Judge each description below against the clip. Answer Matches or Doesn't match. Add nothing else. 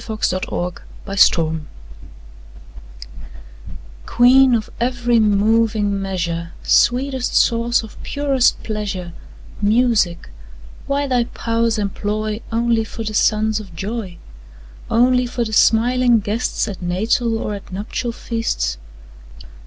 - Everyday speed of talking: Doesn't match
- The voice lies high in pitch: Matches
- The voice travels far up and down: Doesn't match